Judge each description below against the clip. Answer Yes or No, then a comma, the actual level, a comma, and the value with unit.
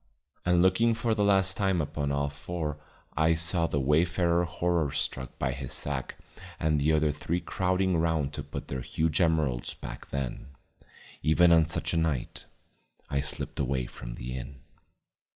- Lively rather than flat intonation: No, average, 3.6 semitones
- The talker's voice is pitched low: Yes, very low, 80 Hz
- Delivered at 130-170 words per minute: Yes, average, 165 wpm